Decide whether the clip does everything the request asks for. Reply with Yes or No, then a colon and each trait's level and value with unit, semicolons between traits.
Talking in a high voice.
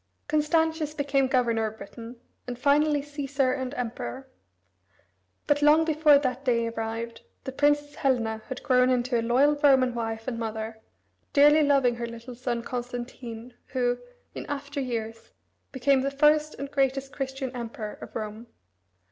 Yes: very high, 255 Hz